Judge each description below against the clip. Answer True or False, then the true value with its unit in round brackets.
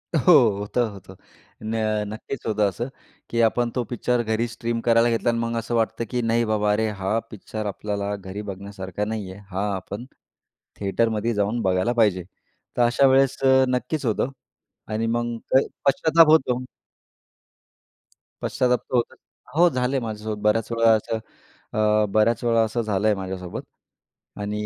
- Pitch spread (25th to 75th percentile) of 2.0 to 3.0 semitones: True (2.5 semitones)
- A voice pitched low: True (110 Hz)